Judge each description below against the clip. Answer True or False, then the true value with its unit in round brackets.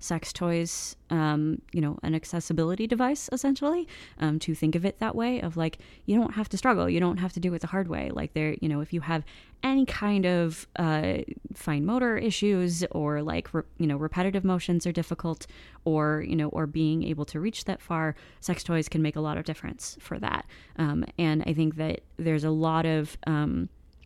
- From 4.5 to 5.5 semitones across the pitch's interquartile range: False (3.5 semitones)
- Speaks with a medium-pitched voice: True (165 Hz)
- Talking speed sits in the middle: False (210 wpm)